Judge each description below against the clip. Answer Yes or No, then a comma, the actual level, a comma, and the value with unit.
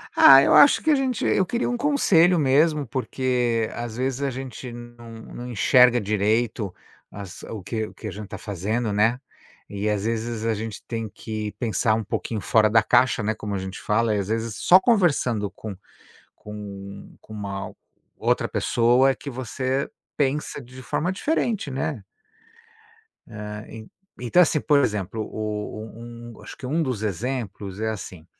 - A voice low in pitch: Yes, low, 115 Hz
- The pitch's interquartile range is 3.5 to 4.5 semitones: Yes, average, 3.9 semitones